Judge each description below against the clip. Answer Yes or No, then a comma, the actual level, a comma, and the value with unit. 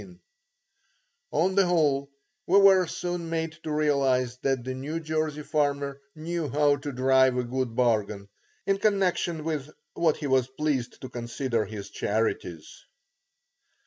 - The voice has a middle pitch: Yes, medium, 145 Hz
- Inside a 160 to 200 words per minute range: No, average, 140 wpm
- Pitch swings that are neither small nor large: Yes, average, 4.0 semitones